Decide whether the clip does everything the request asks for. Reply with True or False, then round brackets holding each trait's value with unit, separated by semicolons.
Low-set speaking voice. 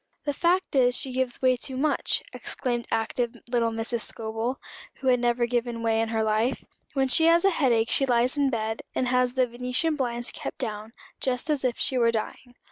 False (245 Hz)